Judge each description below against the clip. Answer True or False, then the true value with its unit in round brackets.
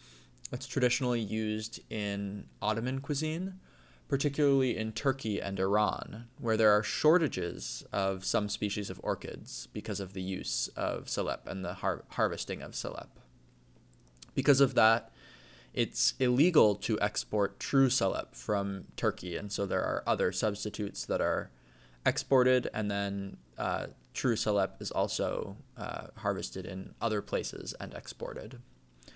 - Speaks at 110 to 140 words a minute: True (135 wpm)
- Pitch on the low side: True (105 Hz)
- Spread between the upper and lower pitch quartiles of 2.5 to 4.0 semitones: False (4.8 semitones)